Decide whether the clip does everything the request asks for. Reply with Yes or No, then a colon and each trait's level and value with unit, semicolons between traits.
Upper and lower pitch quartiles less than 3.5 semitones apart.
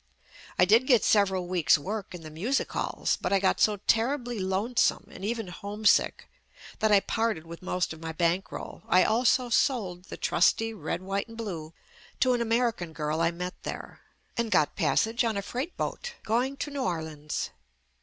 No: average, 4.9 semitones